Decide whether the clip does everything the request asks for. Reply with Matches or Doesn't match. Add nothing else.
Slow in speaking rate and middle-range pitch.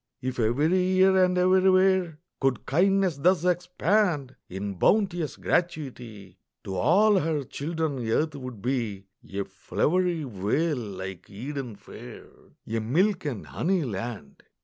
Matches